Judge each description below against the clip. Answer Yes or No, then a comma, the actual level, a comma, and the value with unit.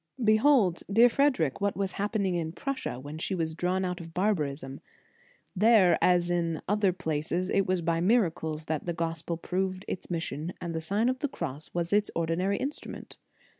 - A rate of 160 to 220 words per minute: Yes, average, 180 wpm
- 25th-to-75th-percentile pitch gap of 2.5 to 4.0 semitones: Yes, average, 3.7 semitones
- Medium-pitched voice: Yes, medium, 180 Hz